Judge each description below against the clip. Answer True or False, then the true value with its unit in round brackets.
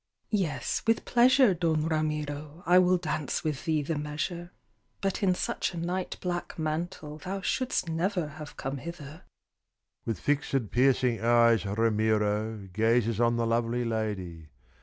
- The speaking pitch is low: False (150 Hz)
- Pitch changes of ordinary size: False (6.8 semitones)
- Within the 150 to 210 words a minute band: False (140 wpm)